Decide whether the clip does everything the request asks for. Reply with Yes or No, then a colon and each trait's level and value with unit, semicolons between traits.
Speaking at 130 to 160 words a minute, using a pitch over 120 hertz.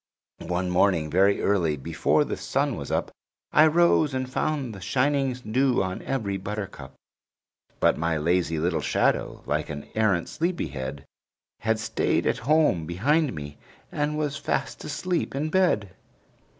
No: average, 150 wpm; low, 105 Hz